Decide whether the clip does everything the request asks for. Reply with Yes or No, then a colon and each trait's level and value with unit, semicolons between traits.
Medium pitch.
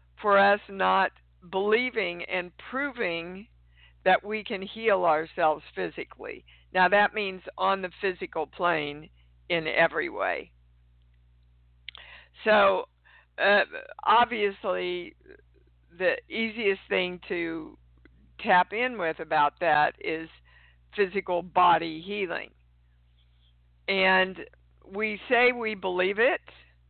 Yes: medium, 175 Hz